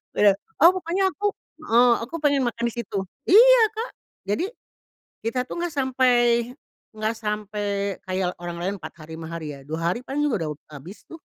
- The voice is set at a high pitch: Yes, high, 225 Hz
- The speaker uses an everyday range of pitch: No, wide, 7.5 semitones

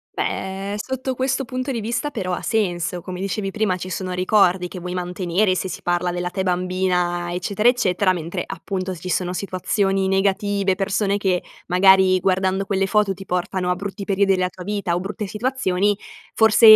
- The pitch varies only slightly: Yes, narrow, 2.0 semitones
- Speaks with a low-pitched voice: No, high, 190 Hz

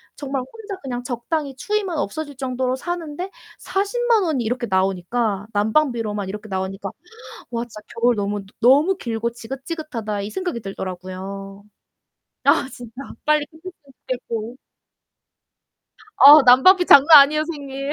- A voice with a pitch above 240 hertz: Yes, very high, 255 Hz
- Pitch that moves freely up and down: Yes, wide, 6.3 semitones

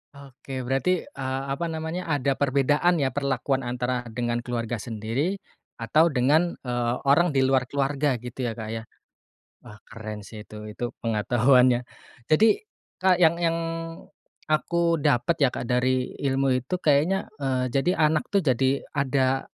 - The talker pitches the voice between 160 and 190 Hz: No, low, 135 Hz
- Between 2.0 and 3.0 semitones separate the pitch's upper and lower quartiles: No, average, 3.8 semitones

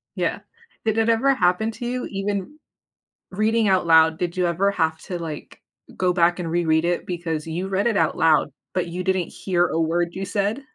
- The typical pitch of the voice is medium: Yes, medium, 180 Hz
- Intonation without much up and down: No, average, 3.1 semitones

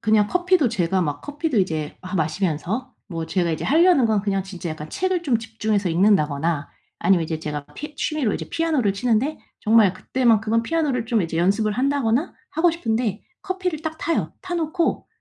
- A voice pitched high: Yes, high, 220 Hz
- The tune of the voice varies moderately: No, wide, 8.5 semitones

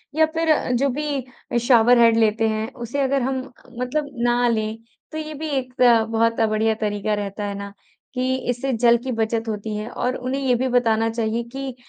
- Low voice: No, high, 240 Hz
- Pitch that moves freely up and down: No, average, 2.9 semitones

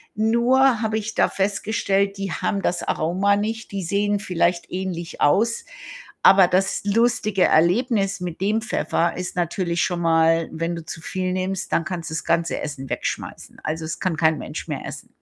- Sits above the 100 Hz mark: Yes, medium, 185 Hz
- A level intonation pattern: No, average, 3.4 semitones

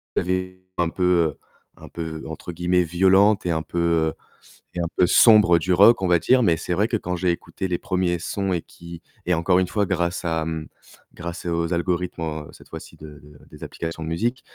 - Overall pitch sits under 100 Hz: Yes, very low, 85 Hz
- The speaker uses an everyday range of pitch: No, narrow, 1.9 semitones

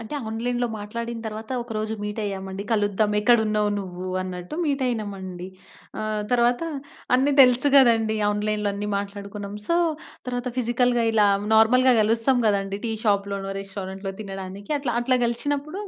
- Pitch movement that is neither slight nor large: Yes, average, 3.3 semitones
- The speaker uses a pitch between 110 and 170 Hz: No, high, 215 Hz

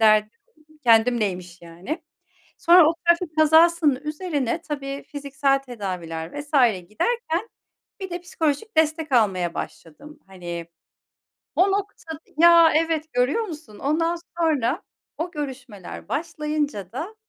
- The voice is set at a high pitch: Yes, very high, 295 Hz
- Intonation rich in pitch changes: Yes, wide, 6.9 semitones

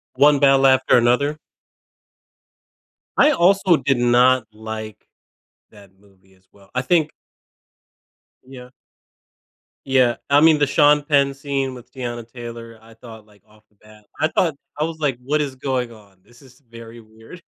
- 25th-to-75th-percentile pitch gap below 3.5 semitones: No, average, 4.2 semitones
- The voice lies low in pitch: Yes, low, 125 Hz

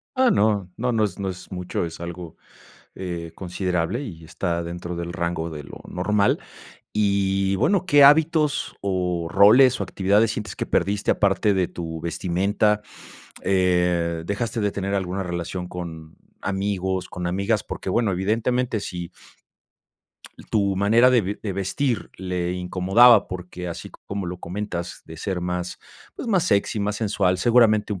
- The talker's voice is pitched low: Yes, very low, 95 Hz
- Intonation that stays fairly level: No, average, 3.0 semitones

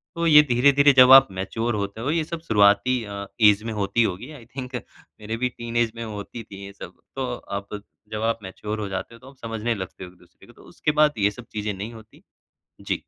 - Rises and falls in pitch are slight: No, average, 3.8 semitones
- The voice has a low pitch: Yes, low, 115 Hz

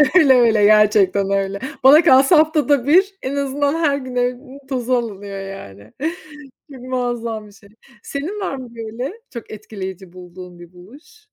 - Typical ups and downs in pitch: No, wide, 5.9 semitones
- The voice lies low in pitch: No, high, 240 Hz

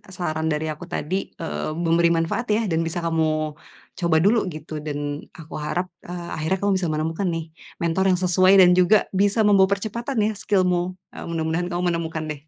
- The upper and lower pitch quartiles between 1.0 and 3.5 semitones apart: Yes, average, 2.9 semitones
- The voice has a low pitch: No, medium, 170 Hz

